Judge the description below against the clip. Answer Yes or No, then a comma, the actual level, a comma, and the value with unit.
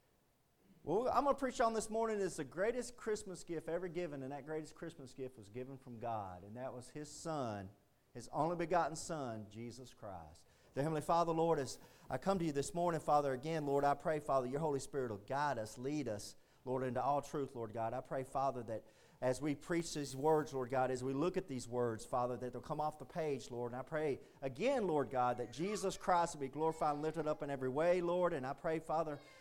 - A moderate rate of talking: No, fast, 230 wpm